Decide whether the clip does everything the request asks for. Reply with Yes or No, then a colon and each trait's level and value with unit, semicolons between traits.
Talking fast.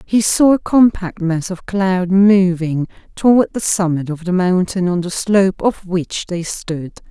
No: average, 175 wpm